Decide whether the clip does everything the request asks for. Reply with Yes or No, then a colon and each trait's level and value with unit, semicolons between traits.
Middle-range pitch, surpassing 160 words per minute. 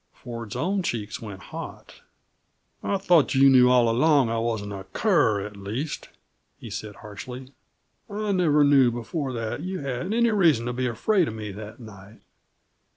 No: low, 125 Hz; average, 170 wpm